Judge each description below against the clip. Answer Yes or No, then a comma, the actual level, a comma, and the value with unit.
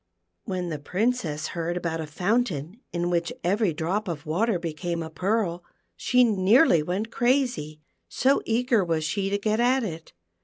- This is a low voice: No, medium, 180 Hz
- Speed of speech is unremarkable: Yes, average, 160 wpm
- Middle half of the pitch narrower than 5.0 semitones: No, wide, 5.4 semitones